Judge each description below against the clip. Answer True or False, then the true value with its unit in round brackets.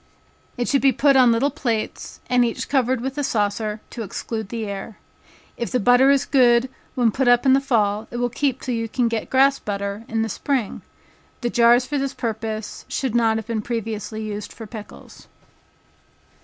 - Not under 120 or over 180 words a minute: False (195 wpm)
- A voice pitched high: True (235 Hz)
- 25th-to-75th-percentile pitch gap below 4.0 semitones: True (3.0 semitones)